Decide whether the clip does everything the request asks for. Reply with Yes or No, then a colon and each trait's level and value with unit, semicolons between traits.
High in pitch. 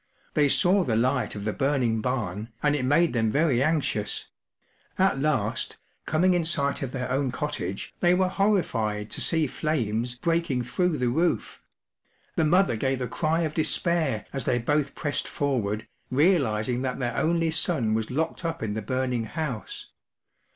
No: low, 135 Hz